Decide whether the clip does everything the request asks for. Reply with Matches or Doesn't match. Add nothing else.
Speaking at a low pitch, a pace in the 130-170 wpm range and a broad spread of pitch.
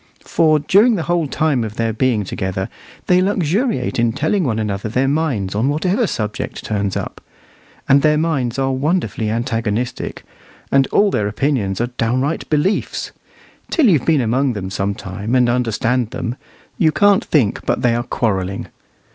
Matches